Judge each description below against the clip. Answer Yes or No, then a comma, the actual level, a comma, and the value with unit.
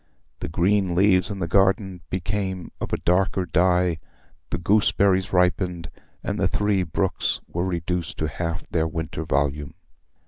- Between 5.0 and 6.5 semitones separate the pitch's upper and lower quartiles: No, narrow, 2.4 semitones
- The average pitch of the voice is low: Yes, very low, 90 Hz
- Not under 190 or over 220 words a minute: No, average, 145 wpm